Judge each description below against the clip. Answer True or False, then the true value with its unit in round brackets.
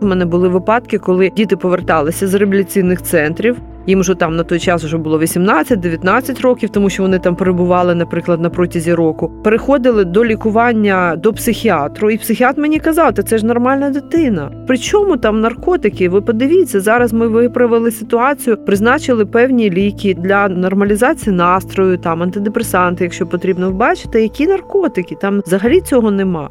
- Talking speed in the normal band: False (160 wpm)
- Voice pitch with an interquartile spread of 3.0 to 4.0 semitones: False (4.5 semitones)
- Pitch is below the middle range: False (205 Hz)